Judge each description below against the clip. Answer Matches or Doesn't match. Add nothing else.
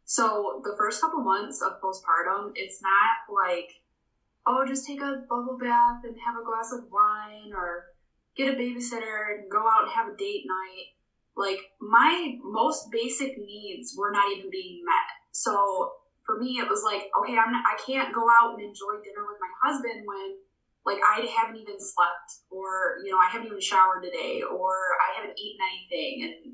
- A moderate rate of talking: Matches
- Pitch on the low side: Doesn't match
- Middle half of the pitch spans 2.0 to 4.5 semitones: Doesn't match